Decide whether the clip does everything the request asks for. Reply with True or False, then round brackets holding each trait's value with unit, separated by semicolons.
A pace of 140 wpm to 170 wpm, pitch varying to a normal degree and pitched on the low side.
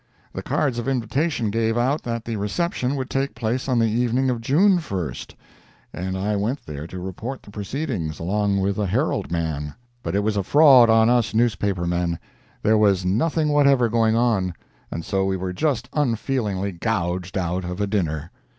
False (180 wpm; 4.9 semitones; 110 Hz)